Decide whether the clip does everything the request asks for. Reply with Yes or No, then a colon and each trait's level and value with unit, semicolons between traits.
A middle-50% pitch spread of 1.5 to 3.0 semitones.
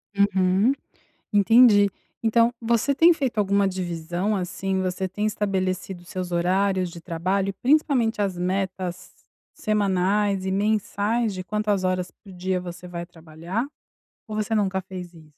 Yes: narrow, 2.6 semitones